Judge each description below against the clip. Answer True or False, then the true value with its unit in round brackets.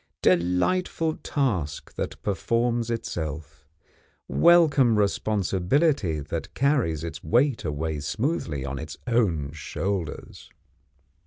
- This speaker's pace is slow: True (90 wpm)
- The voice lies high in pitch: False (95 Hz)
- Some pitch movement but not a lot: False (7.9 semitones)